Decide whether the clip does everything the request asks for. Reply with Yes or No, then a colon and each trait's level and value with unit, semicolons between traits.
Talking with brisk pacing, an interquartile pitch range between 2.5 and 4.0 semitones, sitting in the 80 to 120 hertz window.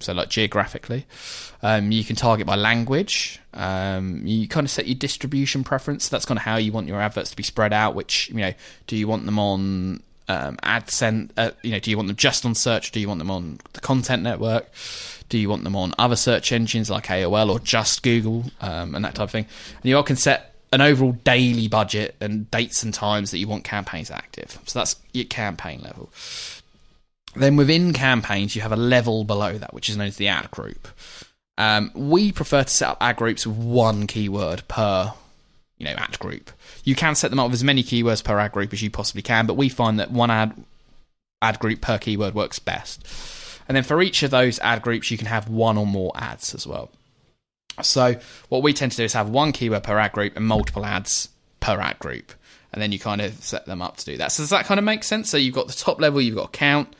Yes: fast, 235 wpm; average, 3.5 semitones; low, 110 Hz